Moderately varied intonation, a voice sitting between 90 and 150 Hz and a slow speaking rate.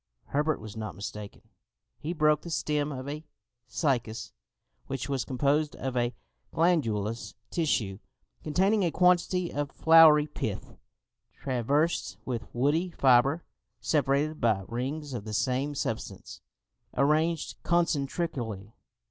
Yes: average, 4.7 semitones; medium, 140 Hz; slow, 115 wpm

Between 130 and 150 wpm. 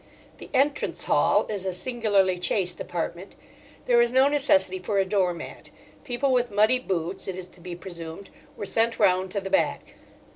No: average, 180 wpm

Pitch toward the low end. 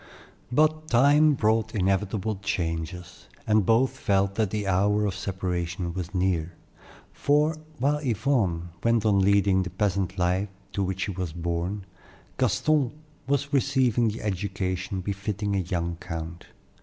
Yes: low, 100 Hz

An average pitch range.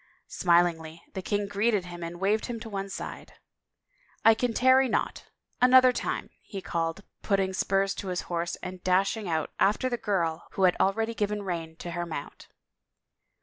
Yes: average, 4.1 semitones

